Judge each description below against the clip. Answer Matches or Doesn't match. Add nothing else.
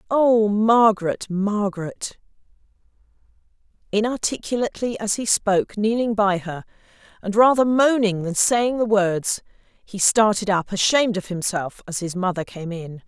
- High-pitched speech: Matches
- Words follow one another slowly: Matches